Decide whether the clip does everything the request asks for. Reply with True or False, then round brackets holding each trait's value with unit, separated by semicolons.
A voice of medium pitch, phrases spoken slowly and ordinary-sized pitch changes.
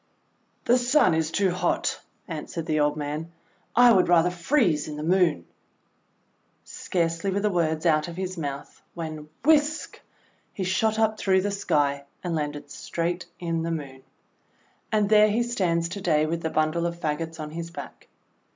False (170 Hz; 170 wpm; 3.9 semitones)